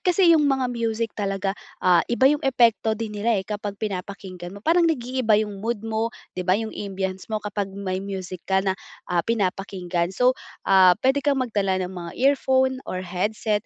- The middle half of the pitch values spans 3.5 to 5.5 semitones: Yes, average, 4.1 semitones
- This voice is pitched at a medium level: No, high, 210 Hz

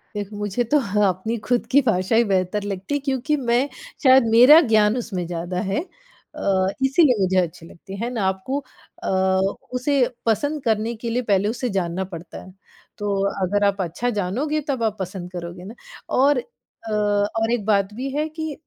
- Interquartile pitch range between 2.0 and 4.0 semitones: No, average, 4.8 semitones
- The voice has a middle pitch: No, high, 210 Hz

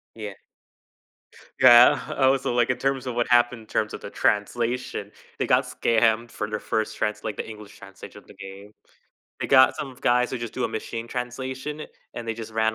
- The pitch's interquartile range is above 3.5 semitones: No, narrow, 2.6 semitones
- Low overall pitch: Yes, low, 115 Hz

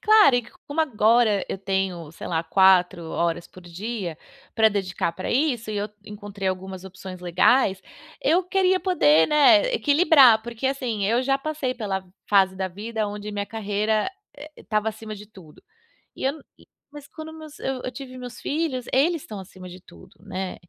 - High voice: Yes, high, 215 Hz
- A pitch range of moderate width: No, wide, 6.1 semitones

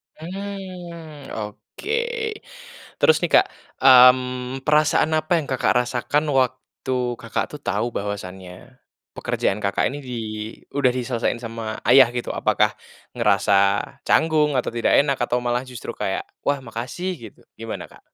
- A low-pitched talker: Yes, low, 125 Hz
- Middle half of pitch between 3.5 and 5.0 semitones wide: Yes, average, 4.2 semitones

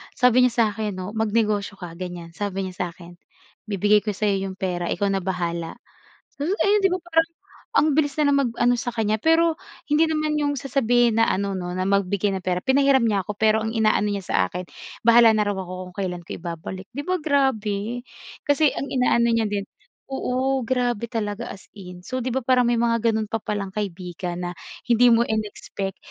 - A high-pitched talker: Yes, high, 215 Hz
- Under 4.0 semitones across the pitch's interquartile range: No, average, 4.7 semitones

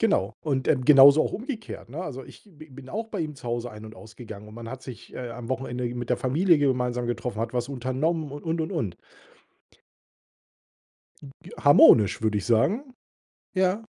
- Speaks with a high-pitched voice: No, low, 130 Hz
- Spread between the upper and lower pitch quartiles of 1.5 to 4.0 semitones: No, average, 4.8 semitones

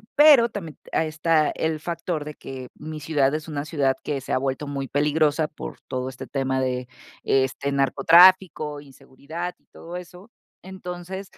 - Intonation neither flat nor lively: Yes, average, 4.0 semitones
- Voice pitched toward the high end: No, medium, 150 Hz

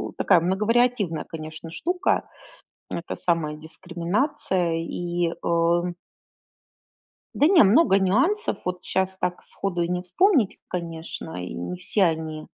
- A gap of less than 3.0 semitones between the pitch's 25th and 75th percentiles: No, average, 3.7 semitones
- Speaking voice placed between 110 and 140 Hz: No, medium, 175 Hz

